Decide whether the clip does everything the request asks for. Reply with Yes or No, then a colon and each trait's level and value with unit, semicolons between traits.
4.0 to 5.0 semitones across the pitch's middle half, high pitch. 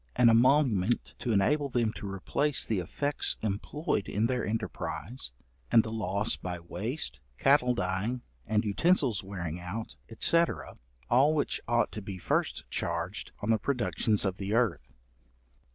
No: average, 4.5 semitones; low, 110 Hz